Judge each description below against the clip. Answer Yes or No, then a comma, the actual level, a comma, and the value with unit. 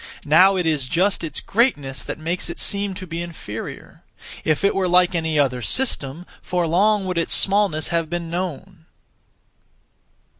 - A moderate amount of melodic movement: Yes, average, 3.3 semitones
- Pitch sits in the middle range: Yes, medium, 170 Hz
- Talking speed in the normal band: Yes, average, 160 wpm